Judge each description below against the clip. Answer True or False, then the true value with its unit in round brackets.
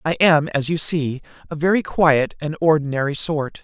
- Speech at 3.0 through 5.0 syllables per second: True (4.8 syllables/s)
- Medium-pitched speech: True (155 Hz)